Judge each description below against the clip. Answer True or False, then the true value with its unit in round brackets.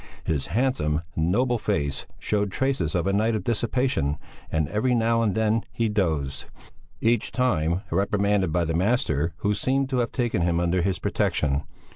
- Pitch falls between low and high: False (100 Hz)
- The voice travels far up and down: True (6.2 semitones)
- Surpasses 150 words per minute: True (165 wpm)